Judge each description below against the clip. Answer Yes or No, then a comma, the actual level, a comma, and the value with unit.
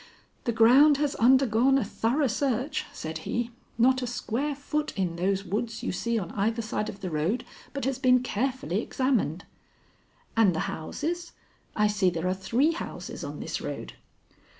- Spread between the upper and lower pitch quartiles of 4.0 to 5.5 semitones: Yes, average, 5.2 semitones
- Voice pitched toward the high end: Yes, high, 235 Hz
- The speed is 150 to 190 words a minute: Yes, average, 170 wpm